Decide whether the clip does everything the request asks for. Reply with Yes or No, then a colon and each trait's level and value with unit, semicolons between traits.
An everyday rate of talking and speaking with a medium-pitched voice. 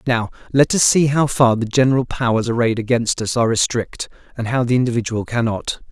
No: average, 195 wpm; low, 120 Hz